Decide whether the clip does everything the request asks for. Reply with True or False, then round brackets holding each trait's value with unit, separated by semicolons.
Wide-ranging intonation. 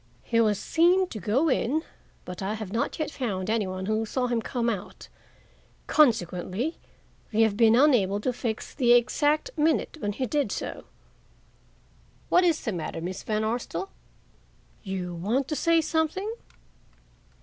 True (6.5 semitones)